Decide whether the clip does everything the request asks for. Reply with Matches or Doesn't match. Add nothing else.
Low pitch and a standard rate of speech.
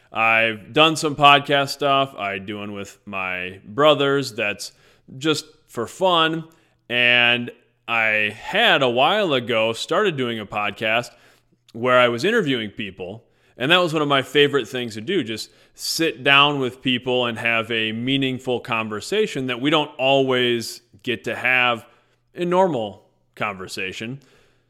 Matches